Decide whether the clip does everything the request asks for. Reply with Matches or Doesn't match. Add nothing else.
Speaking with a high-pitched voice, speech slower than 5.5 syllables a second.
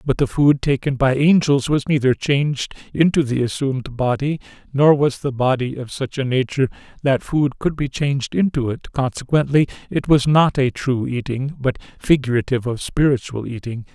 Doesn't match